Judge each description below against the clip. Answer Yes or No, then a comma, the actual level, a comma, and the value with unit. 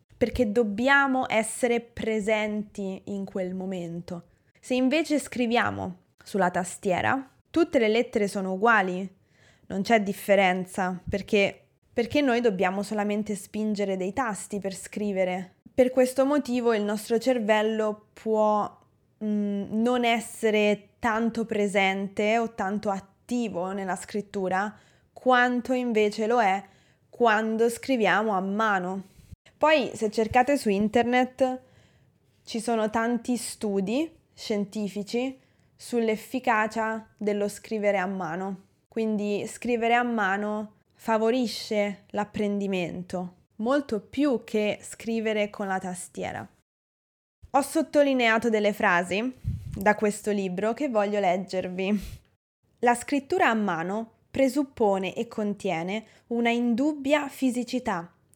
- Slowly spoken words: Yes, slow, 105 wpm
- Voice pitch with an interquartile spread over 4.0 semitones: No, average, 3.2 semitones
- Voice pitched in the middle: No, high, 215 Hz